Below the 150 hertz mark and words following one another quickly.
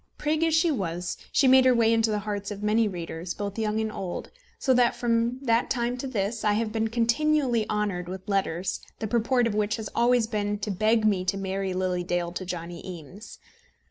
No: high, 215 Hz; fast, 210 wpm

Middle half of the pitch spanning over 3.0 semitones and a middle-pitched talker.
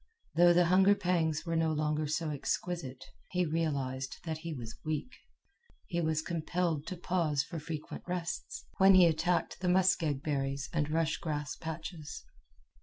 No: average, 2.7 semitones; medium, 160 Hz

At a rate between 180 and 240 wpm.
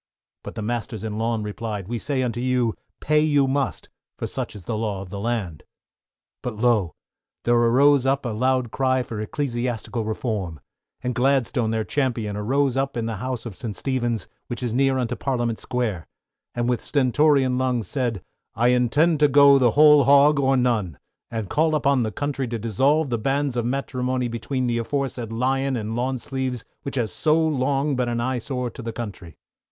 Yes: average, 190 wpm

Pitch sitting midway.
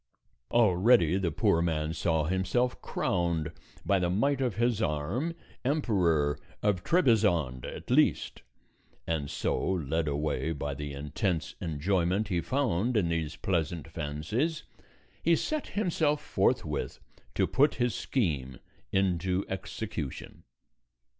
No: very low, 90 Hz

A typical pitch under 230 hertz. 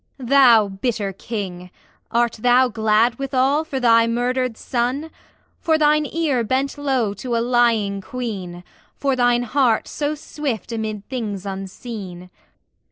No: high, 240 Hz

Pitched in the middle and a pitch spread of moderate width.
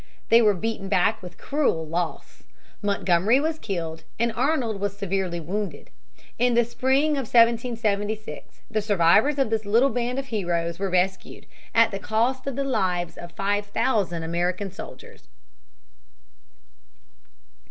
No: high, 210 Hz; average, 4.5 semitones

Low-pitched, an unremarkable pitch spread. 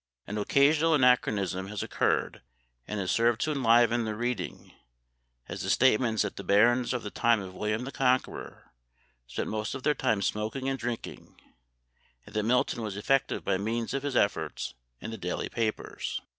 Yes: low, 115 Hz; average, 3.3 semitones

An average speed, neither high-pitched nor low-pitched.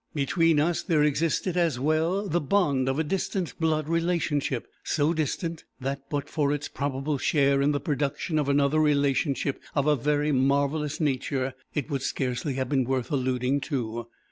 Yes: average, 170 wpm; medium, 145 Hz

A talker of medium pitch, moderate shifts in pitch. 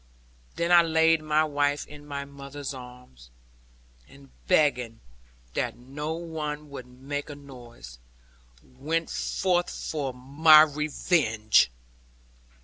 Yes: medium, 145 Hz; average, 3.6 semitones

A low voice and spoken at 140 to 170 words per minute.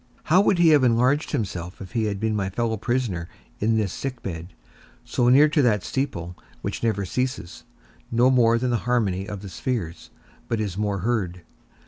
No: low, 110 Hz; average, 185 wpm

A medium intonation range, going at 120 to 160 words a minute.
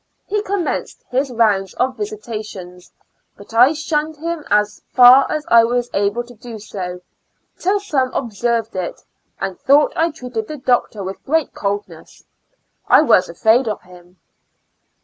No: wide, 6.5 semitones; average, 150 wpm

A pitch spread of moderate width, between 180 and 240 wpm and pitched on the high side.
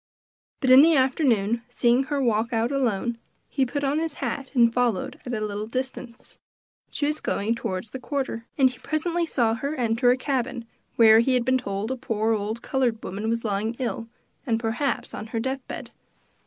Yes: average, 3.0 semitones; average, 190 wpm; high, 240 Hz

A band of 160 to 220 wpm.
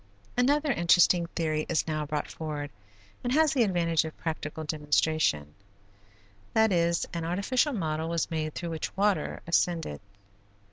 No: average, 140 wpm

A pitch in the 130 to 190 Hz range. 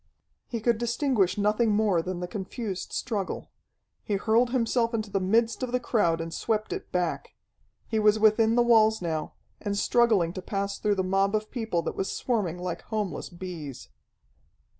No: high, 210 Hz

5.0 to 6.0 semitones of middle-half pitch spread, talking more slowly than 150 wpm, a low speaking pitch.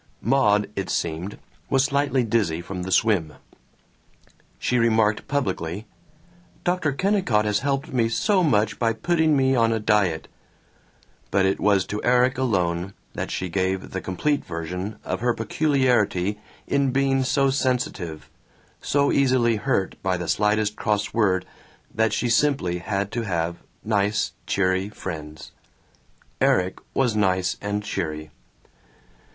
Yes: wide, 5.6 semitones; slow, 135 wpm; low, 105 Hz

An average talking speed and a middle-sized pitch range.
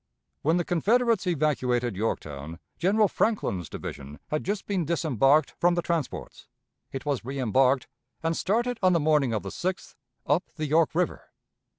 No: average, 155 wpm; wide, 5.9 semitones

